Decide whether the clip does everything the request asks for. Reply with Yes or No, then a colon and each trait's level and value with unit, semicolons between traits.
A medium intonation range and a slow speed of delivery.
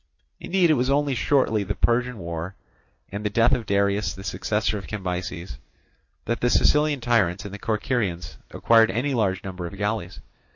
No: average, 4.4 semitones; average, 170 wpm